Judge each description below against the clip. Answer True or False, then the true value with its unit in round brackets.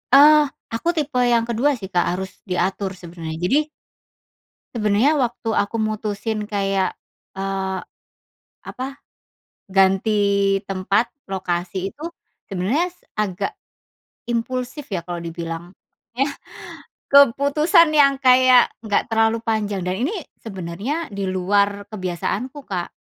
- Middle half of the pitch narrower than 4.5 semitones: False (5.1 semitones)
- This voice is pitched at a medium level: False (210 Hz)